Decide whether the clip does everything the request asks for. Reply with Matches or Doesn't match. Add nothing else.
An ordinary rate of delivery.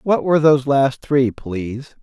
Matches